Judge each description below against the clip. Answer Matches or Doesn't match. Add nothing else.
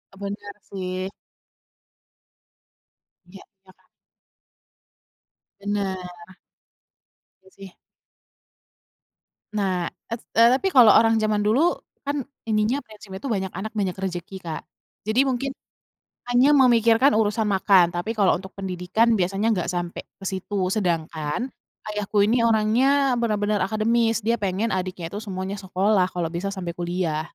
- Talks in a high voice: Matches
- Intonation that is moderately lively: Matches